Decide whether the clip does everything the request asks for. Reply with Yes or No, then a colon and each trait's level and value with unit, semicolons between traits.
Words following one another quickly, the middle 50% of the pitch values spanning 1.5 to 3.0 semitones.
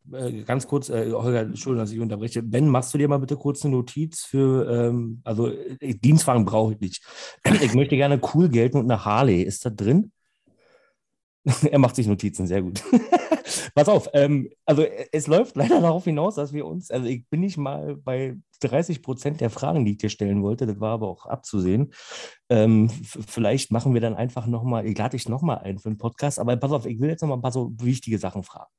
No: fast, 200 wpm; average, 4.3 semitones